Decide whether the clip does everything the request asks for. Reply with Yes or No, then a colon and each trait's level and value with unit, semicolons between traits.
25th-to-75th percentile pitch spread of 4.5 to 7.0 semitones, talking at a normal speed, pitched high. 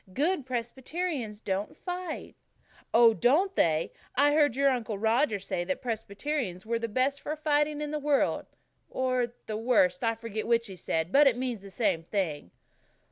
Yes: wide, 5.4 semitones; average, 170 wpm; high, 240 Hz